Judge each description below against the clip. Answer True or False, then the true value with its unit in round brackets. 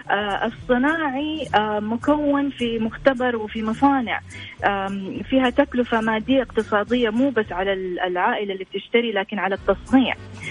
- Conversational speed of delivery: True (110 wpm)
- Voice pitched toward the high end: True (230 Hz)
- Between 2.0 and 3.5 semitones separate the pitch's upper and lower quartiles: False (4.4 semitones)